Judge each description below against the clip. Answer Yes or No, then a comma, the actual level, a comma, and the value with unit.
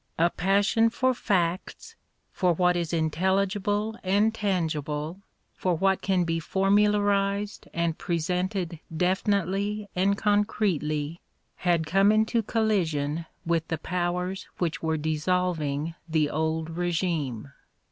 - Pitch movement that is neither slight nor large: Yes, average, 3.6 semitones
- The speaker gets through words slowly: Yes, slow, 115 wpm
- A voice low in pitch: No, medium, 180 Hz